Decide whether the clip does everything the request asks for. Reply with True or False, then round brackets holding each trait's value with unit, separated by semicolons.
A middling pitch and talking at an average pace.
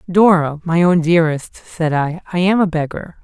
True (170 Hz; 185 wpm)